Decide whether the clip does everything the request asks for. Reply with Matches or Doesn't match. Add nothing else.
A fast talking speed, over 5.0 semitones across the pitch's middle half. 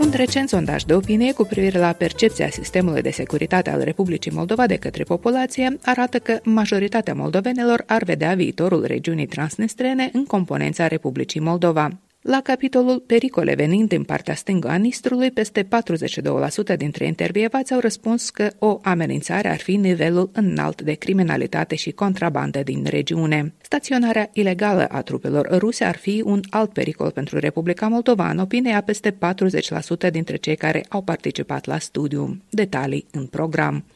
Doesn't match